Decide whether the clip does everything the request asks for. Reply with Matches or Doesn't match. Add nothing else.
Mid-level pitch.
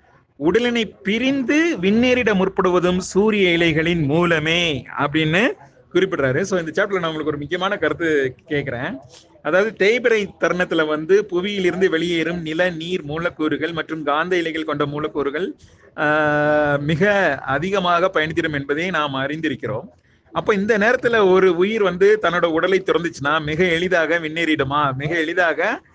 Matches